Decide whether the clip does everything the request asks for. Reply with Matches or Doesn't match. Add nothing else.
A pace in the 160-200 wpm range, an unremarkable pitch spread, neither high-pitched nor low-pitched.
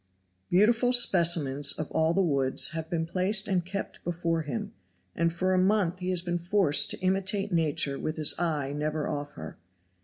Matches